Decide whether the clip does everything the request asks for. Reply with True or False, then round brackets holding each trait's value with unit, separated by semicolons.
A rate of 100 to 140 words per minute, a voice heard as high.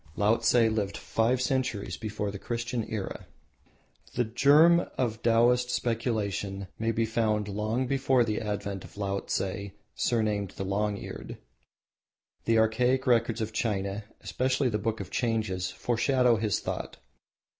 False (135 wpm; 110 Hz)